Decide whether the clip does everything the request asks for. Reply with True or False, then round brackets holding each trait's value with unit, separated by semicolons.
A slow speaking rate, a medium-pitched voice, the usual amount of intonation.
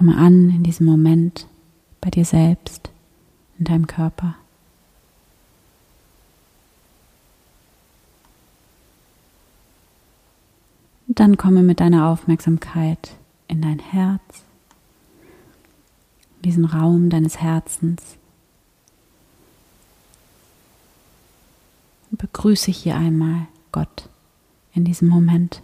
False (75 wpm; 165 Hz; 1.7 semitones)